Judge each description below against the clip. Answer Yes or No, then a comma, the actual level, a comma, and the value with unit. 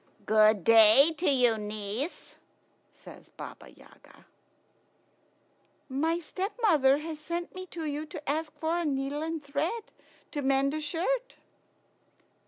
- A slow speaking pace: Yes, slow, 125 wpm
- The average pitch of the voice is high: Yes, very high, 300 Hz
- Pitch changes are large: No, average, 3.6 semitones